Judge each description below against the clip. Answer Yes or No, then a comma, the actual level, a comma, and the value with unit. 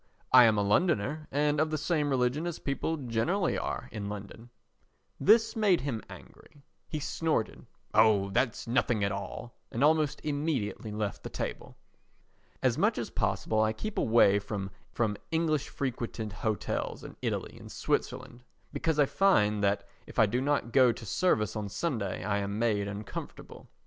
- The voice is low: Yes, low, 120 Hz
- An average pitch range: No, wide, 6.2 semitones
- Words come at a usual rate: Yes, average, 160 wpm